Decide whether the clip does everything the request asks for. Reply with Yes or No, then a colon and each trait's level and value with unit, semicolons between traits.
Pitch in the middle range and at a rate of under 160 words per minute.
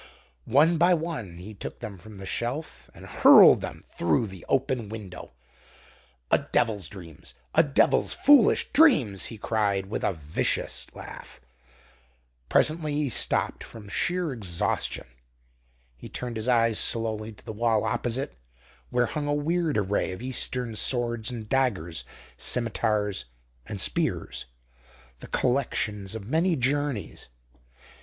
No: low, 115 Hz; slow, 135 wpm